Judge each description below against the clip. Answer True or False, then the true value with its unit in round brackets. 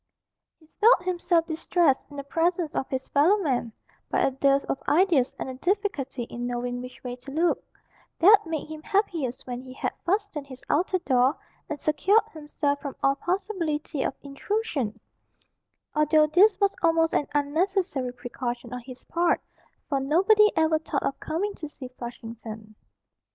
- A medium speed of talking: True (160 wpm)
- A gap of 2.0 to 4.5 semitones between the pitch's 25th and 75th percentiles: False (5.2 semitones)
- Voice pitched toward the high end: True (300 Hz)